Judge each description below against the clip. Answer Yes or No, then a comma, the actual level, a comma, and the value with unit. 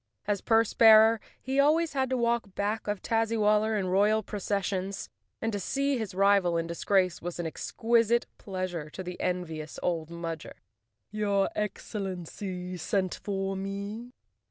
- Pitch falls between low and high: No, high, 200 Hz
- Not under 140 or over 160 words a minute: Yes, average, 150 wpm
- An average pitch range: Yes, average, 3.5 semitones